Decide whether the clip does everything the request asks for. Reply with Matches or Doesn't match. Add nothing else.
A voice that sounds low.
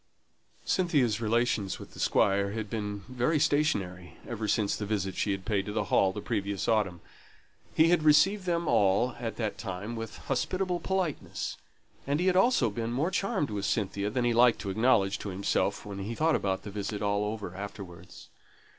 Matches